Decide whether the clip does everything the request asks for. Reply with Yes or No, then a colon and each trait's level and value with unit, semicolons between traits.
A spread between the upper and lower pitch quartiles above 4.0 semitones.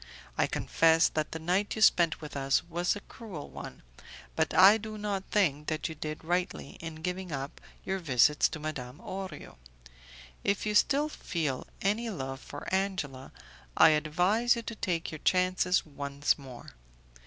Yes: average, 4.5 semitones